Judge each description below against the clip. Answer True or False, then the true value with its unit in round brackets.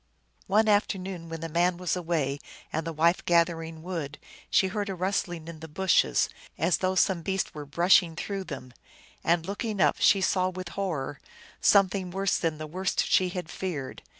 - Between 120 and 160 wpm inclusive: False (180 wpm)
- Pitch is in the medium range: True (175 Hz)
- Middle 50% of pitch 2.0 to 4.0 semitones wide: True (2.8 semitones)